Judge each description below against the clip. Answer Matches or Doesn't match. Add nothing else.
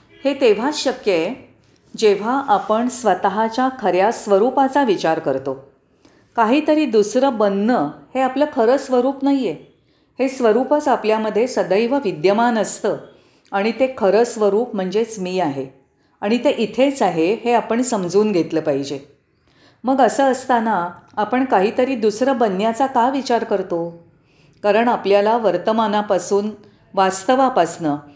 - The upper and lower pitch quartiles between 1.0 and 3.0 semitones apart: Doesn't match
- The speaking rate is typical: Matches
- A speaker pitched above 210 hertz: Matches